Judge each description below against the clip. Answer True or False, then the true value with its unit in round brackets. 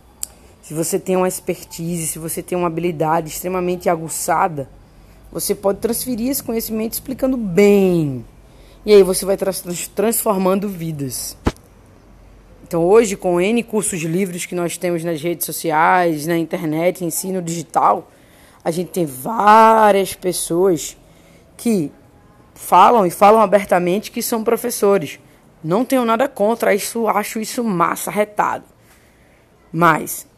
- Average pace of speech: True (130 wpm)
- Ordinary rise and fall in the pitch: True (3.9 semitones)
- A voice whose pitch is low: False (185 Hz)